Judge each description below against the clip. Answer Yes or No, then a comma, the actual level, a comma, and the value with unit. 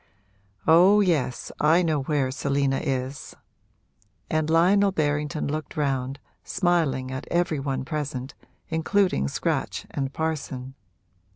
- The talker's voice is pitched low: No, medium, 150 Hz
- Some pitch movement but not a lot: Yes, average, 3.5 semitones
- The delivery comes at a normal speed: No, slow, 110 wpm